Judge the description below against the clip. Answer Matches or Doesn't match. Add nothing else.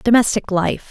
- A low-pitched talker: Doesn't match